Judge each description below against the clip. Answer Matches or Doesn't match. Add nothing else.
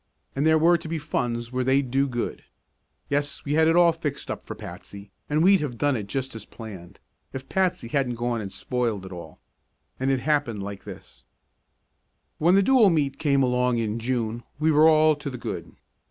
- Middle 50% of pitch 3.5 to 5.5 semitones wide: Matches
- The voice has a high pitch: Doesn't match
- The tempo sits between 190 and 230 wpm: Matches